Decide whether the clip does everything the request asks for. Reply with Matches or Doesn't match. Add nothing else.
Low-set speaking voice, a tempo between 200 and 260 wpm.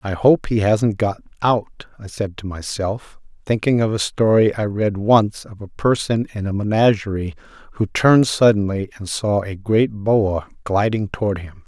Doesn't match